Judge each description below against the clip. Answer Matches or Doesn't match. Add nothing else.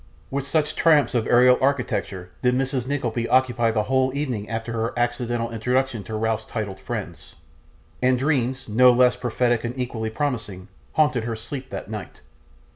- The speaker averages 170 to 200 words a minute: Doesn't match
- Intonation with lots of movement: Doesn't match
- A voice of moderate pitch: Doesn't match